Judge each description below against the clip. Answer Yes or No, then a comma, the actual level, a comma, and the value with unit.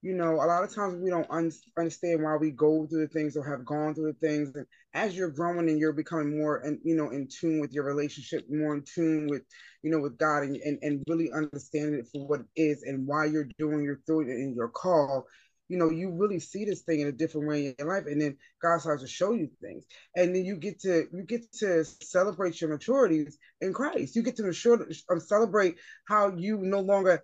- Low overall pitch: No, medium, 160 Hz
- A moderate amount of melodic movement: Yes, average, 3.3 semitones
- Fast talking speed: Yes, fast, 240 wpm